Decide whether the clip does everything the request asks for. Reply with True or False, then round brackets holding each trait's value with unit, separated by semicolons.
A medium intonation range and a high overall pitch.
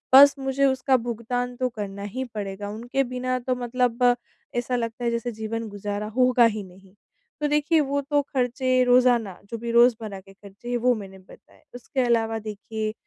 True (3.0 semitones; 240 Hz)